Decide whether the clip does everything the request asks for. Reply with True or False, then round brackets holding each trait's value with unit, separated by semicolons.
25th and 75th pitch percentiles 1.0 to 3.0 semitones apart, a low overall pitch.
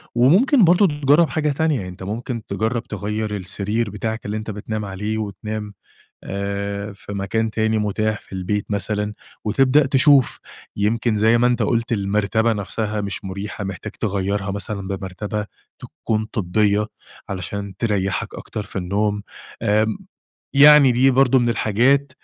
True (2.7 semitones; 105 Hz)